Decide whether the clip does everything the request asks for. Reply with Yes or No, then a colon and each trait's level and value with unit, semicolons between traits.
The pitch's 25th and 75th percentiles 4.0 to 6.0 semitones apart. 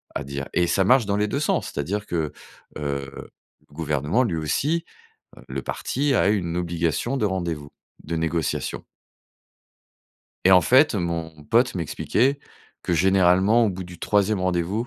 Yes: average, 4.5 semitones